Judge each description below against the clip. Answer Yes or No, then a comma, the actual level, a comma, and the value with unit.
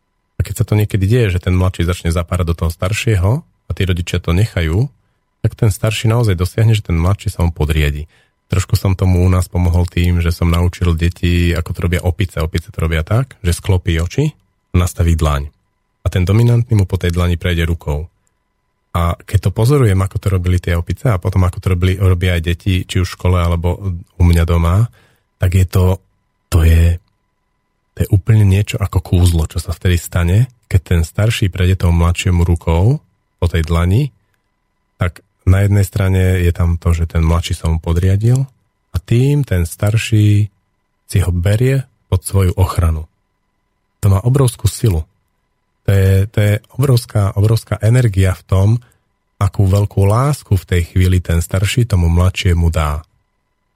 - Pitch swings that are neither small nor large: Yes, average, 3.0 semitones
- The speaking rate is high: Yes, fast, 180 wpm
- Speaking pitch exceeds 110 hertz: No, very low, 95 Hz